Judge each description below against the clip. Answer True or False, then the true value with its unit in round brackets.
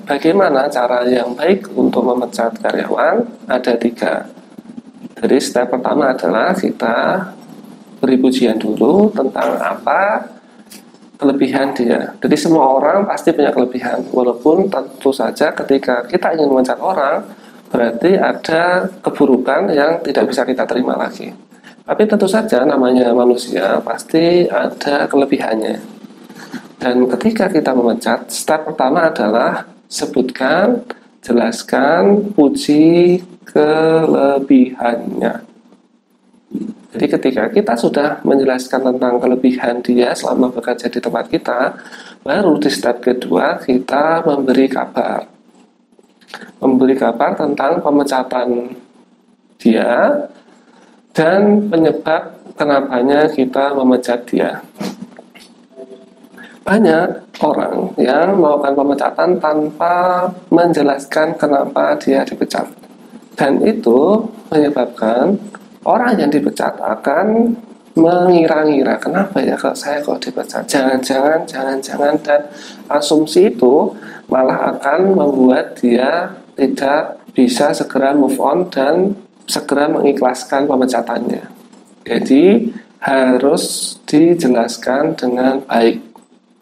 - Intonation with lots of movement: True (6.1 semitones)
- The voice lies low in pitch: False (145 Hz)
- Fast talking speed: False (100 wpm)